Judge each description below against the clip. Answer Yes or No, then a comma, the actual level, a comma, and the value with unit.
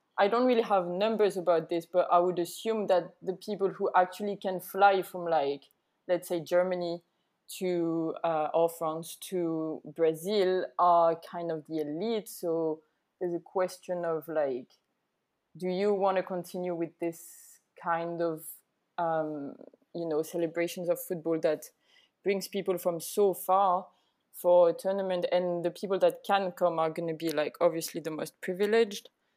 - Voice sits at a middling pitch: Yes, medium, 175 Hz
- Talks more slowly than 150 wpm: No, average, 160 wpm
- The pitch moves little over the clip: Yes, narrow, 2.2 semitones